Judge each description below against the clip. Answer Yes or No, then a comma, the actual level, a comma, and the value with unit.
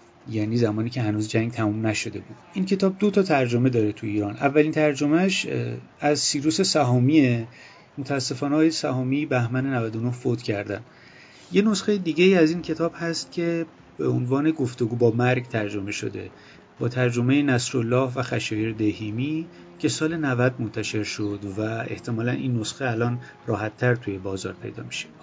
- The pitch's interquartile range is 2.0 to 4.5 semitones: No, wide, 5.5 semitones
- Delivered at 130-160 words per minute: Yes, average, 150 wpm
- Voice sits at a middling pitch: No, low, 125 Hz